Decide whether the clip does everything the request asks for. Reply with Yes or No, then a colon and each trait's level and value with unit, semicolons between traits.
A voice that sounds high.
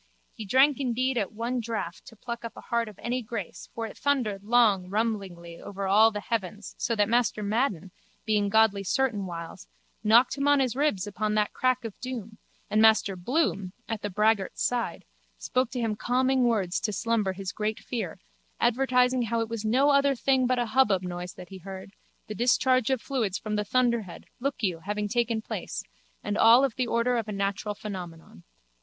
Yes: high, 220 Hz